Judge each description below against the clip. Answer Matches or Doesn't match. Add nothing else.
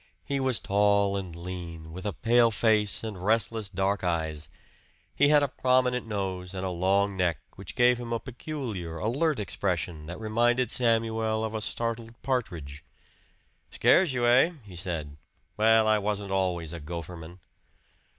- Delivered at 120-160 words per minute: Matches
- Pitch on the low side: Matches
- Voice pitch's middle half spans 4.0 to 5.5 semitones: Matches